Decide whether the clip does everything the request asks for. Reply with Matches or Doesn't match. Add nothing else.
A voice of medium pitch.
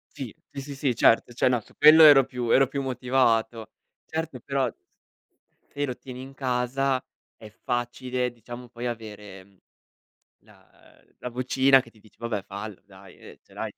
Doesn't match